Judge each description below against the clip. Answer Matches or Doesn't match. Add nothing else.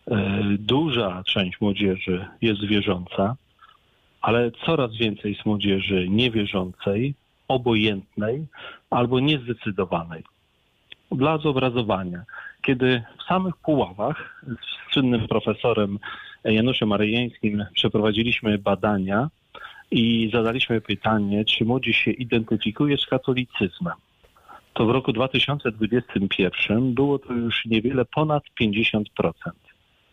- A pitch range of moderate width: Matches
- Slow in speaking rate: Matches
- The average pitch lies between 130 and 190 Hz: Doesn't match